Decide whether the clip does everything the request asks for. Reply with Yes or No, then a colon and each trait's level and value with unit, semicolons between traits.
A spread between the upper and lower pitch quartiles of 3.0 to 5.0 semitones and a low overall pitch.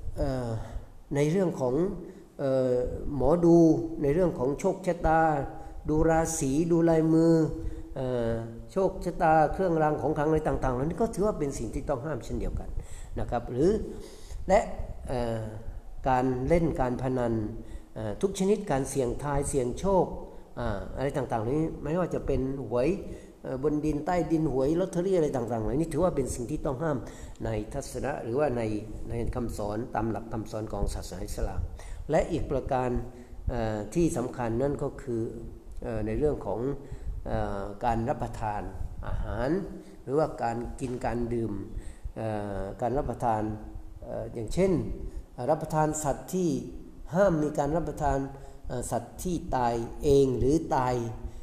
No: wide, 5.4 semitones; low, 130 Hz